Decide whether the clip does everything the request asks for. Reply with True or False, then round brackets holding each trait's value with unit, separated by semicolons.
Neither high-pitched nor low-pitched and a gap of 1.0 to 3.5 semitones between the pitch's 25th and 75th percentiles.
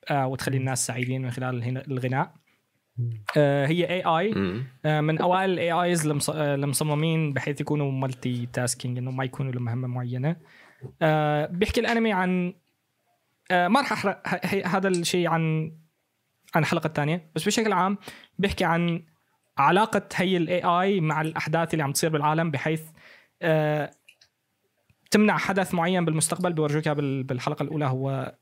False (155 Hz; 4.4 semitones)